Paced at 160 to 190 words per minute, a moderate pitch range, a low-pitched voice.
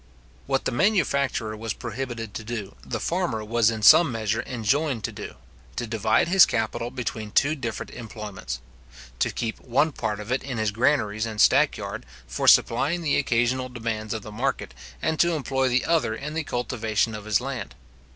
Yes: average, 180 wpm; average, 3.8 semitones; low, 120 Hz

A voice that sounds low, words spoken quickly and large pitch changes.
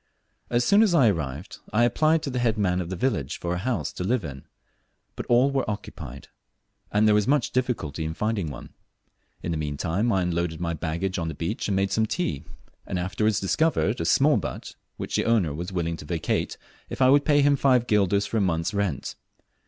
Yes: low, 100 Hz; fast, 215 wpm; wide, 6.4 semitones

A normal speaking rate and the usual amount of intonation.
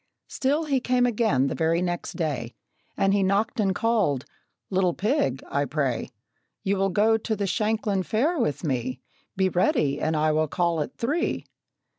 No: average, 170 wpm; wide, 6.4 semitones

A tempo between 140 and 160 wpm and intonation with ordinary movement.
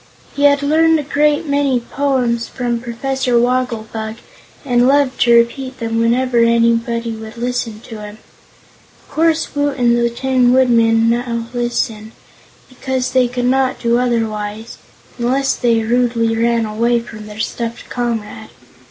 No: average, 145 wpm; narrow, 2.1 semitones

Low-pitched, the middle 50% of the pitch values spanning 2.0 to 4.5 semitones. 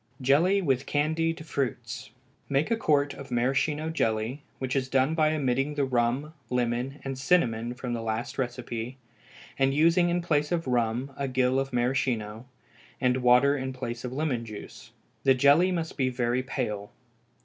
Yes: low, 130 Hz; average, 3.2 semitones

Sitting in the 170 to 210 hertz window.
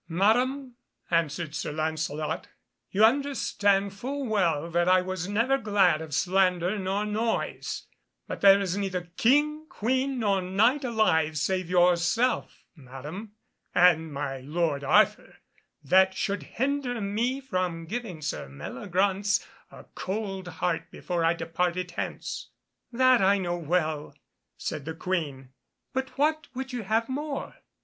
Yes: high, 190 Hz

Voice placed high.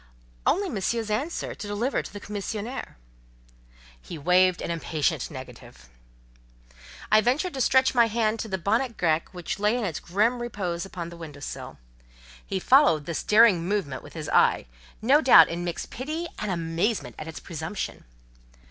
Yes: high, 205 Hz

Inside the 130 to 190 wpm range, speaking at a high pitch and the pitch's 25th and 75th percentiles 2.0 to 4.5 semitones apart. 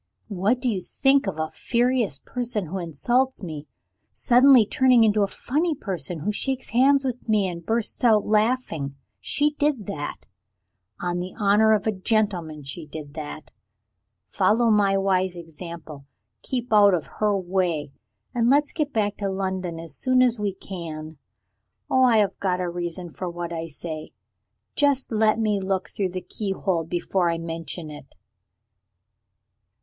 No: average, 160 wpm; high, 195 Hz; wide, 5.5 semitones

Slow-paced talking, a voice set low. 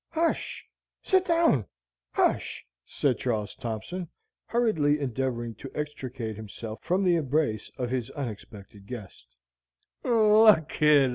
Yes: slow, 100 wpm; low, 130 Hz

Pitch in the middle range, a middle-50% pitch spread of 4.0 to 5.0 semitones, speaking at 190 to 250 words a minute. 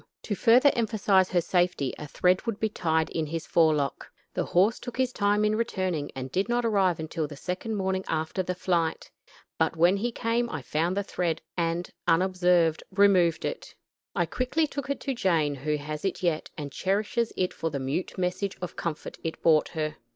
Yes: medium, 180 Hz; average, 4.4 semitones; average, 195 wpm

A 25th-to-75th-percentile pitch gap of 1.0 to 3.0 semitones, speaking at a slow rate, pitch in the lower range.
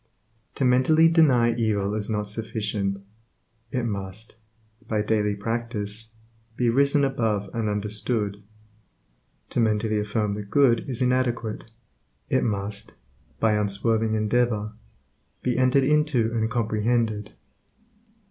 Yes: average, 2.7 semitones; slow, 110 wpm; low, 110 Hz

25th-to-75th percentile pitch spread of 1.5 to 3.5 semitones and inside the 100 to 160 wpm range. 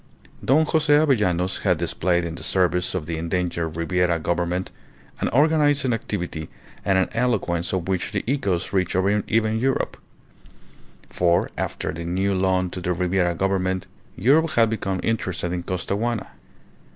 No: average, 4.2 semitones; average, 145 wpm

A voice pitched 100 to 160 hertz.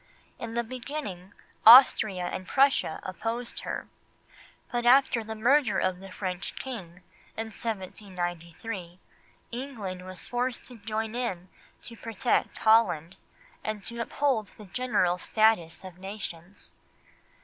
No: high, 215 Hz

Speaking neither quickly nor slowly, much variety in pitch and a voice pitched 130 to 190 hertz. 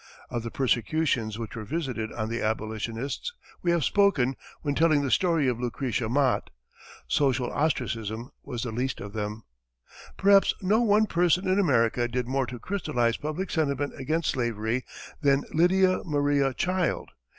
Yes: average, 150 wpm; wide, 5.9 semitones; low, 135 Hz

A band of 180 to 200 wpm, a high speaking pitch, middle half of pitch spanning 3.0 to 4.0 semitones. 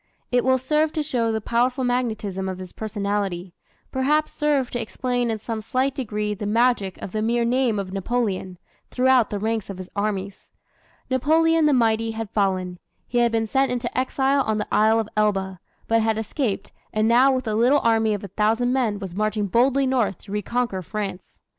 Yes: average, 190 wpm; high, 225 Hz; average, 3.6 semitones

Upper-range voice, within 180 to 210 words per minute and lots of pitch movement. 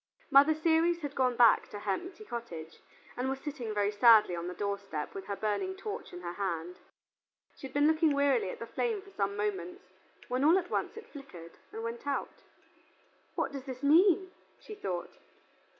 Yes: high, 245 Hz; average, 190 wpm; wide, 7.8 semitones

